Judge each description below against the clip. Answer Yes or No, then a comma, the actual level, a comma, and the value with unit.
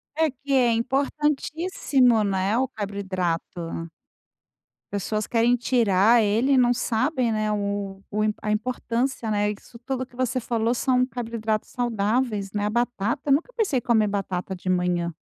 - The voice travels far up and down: No, average, 3.8 semitones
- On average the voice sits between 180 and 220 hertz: No, high, 230 Hz